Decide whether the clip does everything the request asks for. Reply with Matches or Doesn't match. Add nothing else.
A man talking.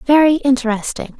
Doesn't match